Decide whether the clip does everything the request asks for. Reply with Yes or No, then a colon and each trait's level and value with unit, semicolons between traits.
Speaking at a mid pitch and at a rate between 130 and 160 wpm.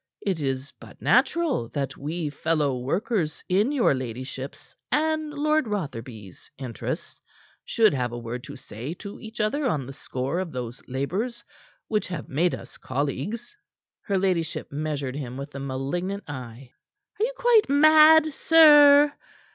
Yes: medium, 160 Hz; average, 145 wpm